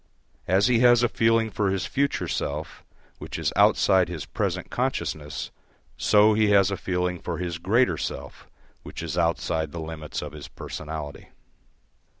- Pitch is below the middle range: Yes, very low, 90 Hz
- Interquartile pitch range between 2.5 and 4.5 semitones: No, average, 5.2 semitones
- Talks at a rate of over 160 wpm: No, average, 155 wpm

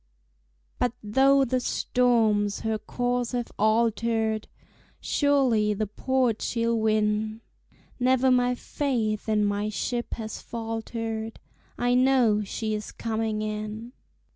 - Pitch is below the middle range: No, high, 225 Hz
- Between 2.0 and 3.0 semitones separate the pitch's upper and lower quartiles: Yes, narrow, 2.5 semitones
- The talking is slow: Yes, slow, 115 wpm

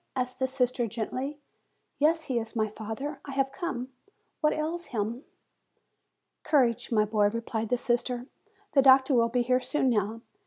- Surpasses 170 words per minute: No, average, 160 wpm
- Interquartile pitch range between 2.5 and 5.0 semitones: Yes, average, 3.0 semitones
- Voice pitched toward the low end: No, very high, 250 Hz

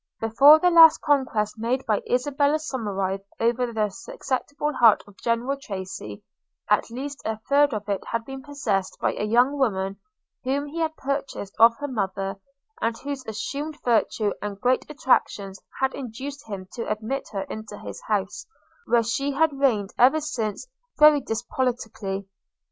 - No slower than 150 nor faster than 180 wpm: Yes, average, 155 wpm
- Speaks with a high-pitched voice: Yes, high, 240 Hz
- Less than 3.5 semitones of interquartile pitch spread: No, average, 5.1 semitones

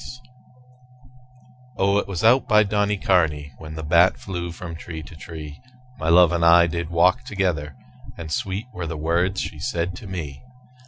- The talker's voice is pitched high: No, very low, 85 Hz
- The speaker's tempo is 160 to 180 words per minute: Yes, average, 170 wpm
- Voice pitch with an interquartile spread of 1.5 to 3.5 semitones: Yes, average, 3.1 semitones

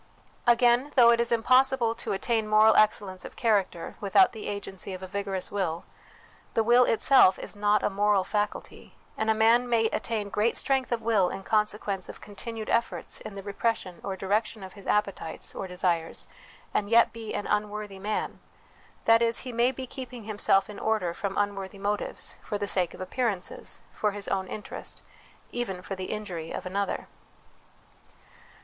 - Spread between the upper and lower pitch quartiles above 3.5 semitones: No, average, 3.0 semitones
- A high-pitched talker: Yes, high, 210 Hz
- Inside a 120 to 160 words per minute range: No, average, 175 wpm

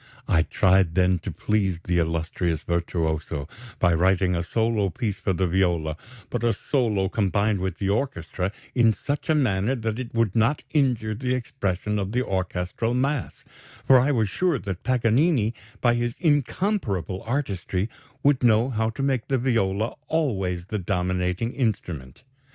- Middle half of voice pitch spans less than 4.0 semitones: No, average, 5.3 semitones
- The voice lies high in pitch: No, low, 105 Hz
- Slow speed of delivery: No, average, 155 wpm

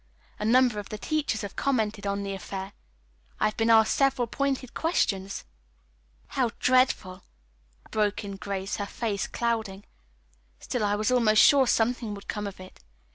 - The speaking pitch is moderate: No, high, 215 Hz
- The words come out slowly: No, average, 155 wpm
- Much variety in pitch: No, average, 3.7 semitones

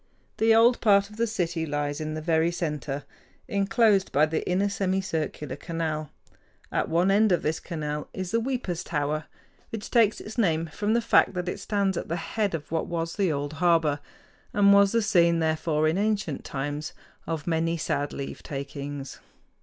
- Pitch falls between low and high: Yes, medium, 170 Hz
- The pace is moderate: Yes, average, 175 wpm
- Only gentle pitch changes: No, average, 4.6 semitones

